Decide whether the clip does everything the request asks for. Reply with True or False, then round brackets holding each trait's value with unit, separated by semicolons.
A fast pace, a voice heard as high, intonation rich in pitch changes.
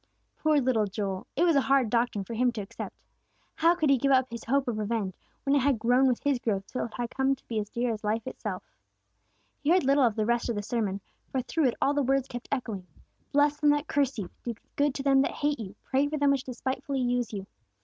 False (250 wpm; 250 Hz; 3.8 semitones)